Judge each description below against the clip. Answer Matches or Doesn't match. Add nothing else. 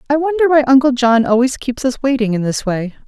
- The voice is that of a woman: Matches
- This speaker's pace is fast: Matches